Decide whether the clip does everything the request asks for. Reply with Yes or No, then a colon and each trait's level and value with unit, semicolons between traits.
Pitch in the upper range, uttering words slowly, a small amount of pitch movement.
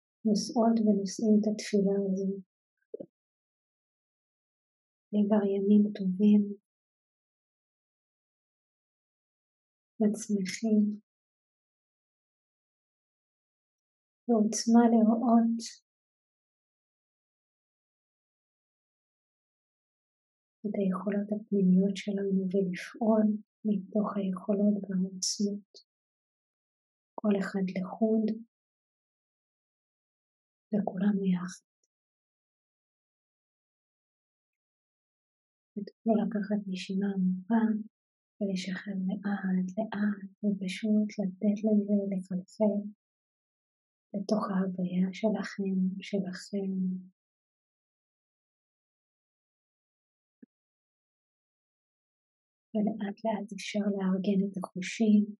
Yes: high, 205 Hz; slow, 50 wpm; narrow, 1.8 semitones